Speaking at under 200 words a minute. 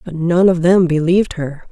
No: fast, 210 wpm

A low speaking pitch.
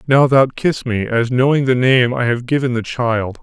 Yes: low, 125 Hz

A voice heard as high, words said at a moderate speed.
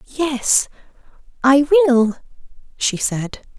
No: very high, 270 Hz; slow, 85 wpm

